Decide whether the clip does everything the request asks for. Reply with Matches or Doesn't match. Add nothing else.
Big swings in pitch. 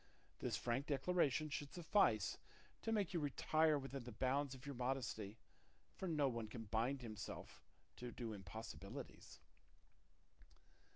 Doesn't match